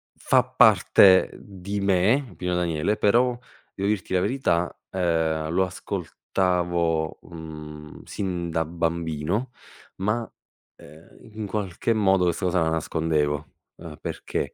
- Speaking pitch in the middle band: No, very low, 90 Hz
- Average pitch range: Yes, average, 3.8 semitones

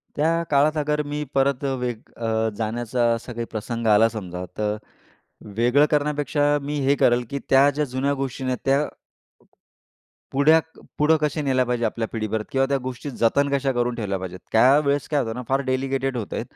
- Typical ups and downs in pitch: Yes, average, 3.7 semitones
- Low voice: Yes, low, 130 Hz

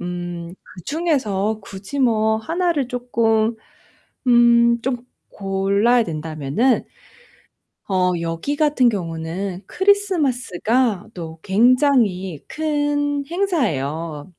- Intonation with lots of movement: Yes, wide, 7.0 semitones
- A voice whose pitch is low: No, high, 220 Hz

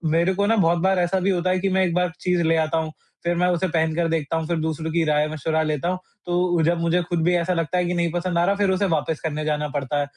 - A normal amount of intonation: No, narrow, 2.1 semitones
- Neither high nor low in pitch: Yes, medium, 170 Hz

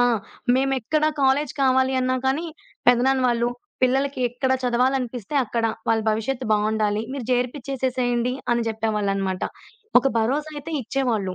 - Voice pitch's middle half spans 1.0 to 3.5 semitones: Yes, average, 2.9 semitones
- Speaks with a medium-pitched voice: No, very high, 250 Hz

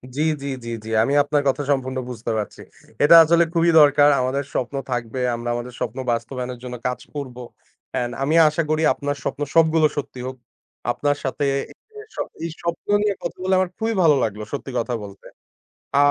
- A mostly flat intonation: No, average, 3.9 semitones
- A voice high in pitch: No, medium, 140 Hz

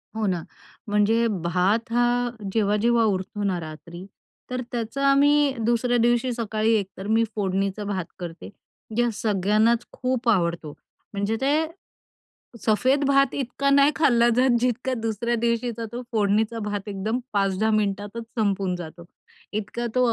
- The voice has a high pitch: Yes, high, 220 Hz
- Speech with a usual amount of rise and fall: Yes, average, 3.3 semitones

